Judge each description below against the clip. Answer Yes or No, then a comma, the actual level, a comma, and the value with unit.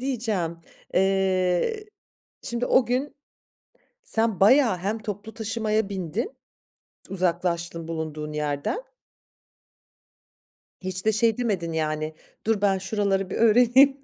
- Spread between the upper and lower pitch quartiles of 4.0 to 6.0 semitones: Yes, average, 4.8 semitones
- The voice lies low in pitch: No, high, 195 Hz